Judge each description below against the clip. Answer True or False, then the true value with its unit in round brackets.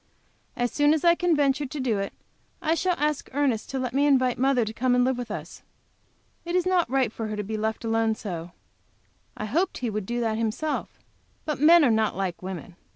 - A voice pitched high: True (250 Hz)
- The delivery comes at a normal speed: False (220 wpm)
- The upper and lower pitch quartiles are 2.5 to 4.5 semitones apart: False (5.1 semitones)